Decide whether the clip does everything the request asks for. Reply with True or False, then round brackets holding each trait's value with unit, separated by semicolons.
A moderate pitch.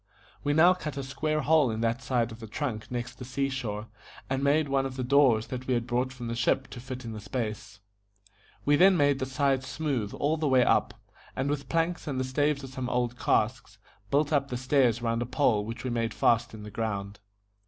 False (130 Hz)